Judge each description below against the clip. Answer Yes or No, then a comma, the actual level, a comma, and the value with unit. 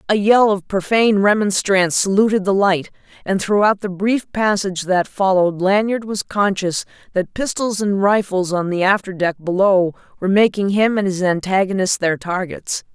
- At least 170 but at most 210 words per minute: No, average, 160 wpm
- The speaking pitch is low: No, high, 195 Hz